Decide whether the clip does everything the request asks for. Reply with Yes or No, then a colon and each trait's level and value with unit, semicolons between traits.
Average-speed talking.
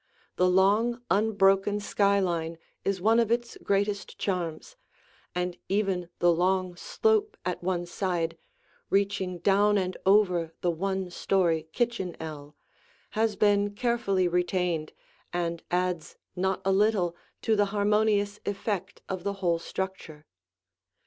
No: slow, 125 wpm